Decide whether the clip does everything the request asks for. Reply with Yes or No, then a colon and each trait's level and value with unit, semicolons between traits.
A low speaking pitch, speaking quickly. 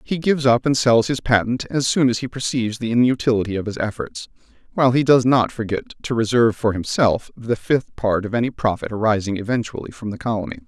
Yes: low, 115 Hz; fast, 210 wpm